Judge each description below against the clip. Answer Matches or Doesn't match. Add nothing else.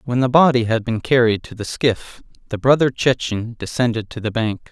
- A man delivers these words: Matches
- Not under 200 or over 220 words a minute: Matches